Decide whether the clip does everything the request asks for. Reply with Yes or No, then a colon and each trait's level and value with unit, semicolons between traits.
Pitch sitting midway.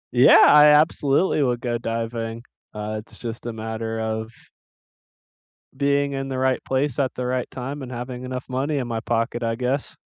No: low, 125 Hz